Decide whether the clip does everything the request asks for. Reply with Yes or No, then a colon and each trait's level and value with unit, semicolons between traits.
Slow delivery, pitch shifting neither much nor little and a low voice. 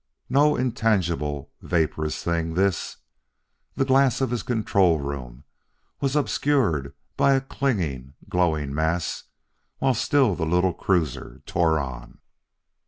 No: slow, 115 wpm; wide, 8.7 semitones; very low, 90 Hz